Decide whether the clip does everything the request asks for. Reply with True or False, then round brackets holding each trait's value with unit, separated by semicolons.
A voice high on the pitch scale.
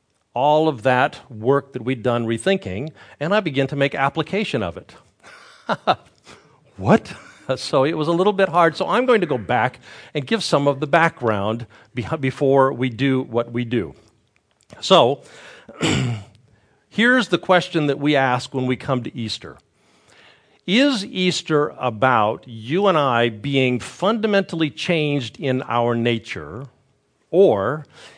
False (135 Hz)